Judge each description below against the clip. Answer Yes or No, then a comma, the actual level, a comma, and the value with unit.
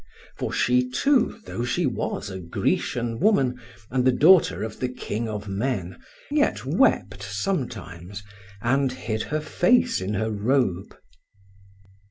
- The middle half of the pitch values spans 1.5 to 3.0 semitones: No, average, 4.9 semitones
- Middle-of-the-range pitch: No, low, 125 Hz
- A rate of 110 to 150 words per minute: Yes, slow, 135 wpm